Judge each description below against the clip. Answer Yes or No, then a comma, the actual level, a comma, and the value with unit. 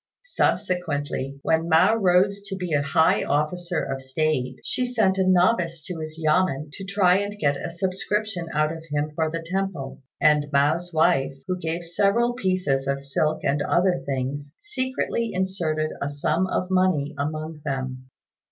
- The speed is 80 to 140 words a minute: No, average, 160 wpm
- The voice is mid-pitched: Yes, medium, 165 Hz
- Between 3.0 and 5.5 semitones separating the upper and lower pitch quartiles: Yes, average, 4.4 semitones